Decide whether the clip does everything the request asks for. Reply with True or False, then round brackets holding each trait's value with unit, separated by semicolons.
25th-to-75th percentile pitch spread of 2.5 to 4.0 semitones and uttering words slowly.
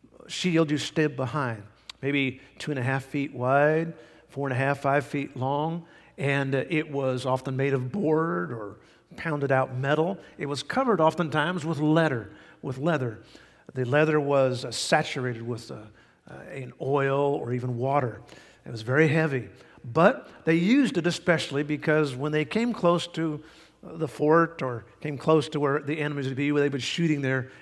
False (3.1 semitones; 180 wpm)